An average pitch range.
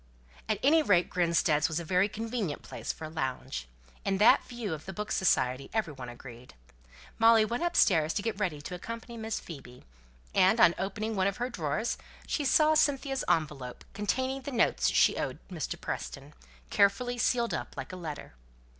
No: wide, 6.7 semitones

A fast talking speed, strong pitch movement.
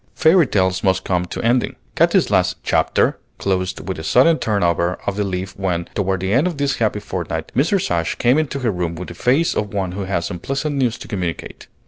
Yes: fast, 215 wpm; wide, 5.9 semitones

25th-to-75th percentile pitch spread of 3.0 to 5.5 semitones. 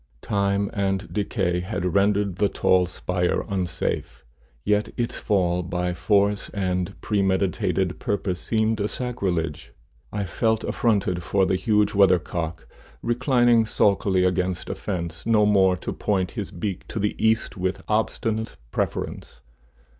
No: narrow, 2.6 semitones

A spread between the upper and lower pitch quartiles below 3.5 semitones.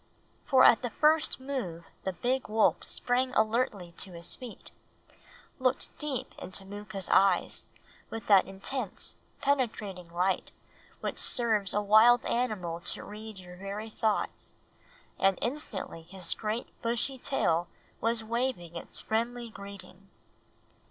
No: average, 4.2 semitones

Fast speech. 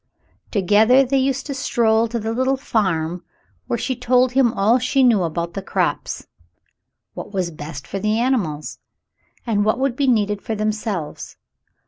No: average, 165 wpm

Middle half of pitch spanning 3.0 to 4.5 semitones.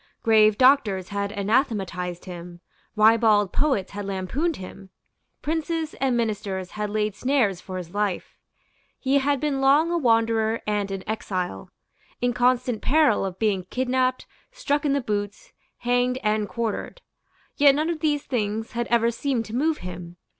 No: average, 5.1 semitones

